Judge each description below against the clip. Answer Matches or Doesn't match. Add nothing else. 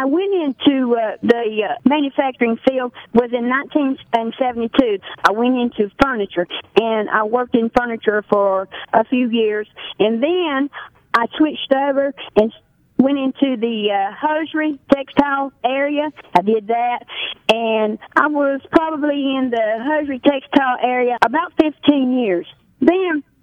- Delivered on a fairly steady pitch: Doesn't match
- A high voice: Matches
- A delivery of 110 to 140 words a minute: Matches